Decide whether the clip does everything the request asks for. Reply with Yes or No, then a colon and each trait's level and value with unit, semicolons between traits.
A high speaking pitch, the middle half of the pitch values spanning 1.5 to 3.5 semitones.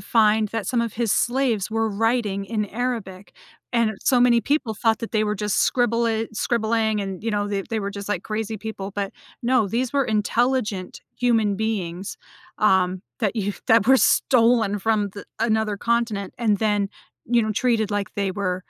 Yes: high, 220 Hz; narrow, 2.5 semitones